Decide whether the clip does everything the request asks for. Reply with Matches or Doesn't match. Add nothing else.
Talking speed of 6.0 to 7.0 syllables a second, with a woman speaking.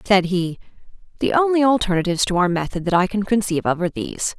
Matches